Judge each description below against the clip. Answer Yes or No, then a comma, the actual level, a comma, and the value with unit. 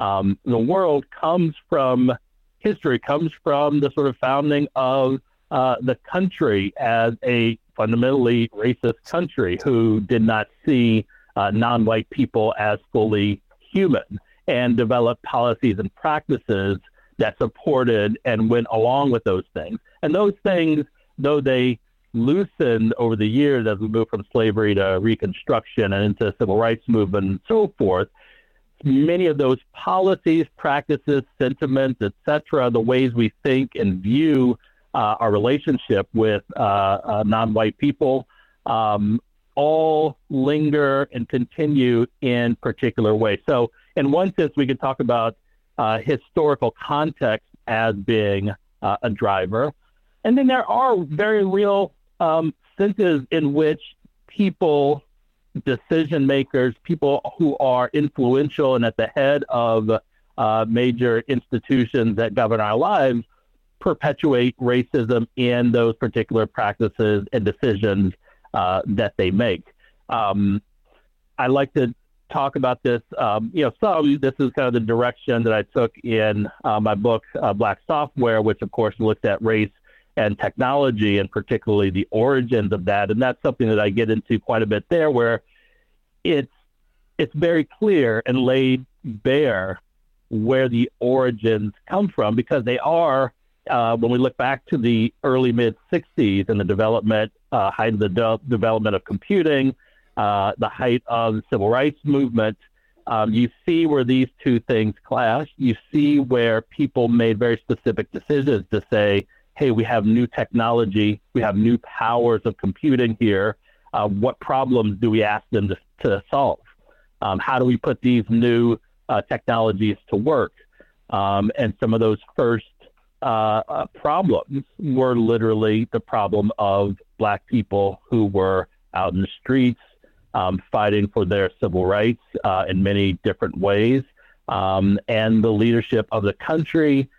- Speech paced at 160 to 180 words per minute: No, average, 150 wpm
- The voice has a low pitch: Yes, low, 120 Hz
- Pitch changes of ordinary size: Yes, average, 4.0 semitones